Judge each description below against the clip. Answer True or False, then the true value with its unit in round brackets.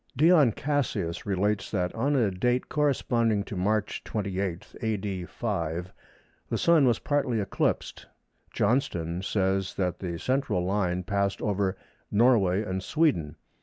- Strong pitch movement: False (4.8 semitones)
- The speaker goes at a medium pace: False (130 wpm)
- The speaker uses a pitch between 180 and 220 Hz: False (100 Hz)